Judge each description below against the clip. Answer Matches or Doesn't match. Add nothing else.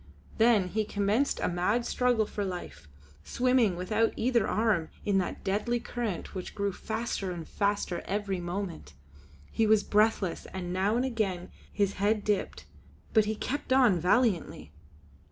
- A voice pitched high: Matches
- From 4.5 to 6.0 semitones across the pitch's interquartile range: Doesn't match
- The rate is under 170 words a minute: Matches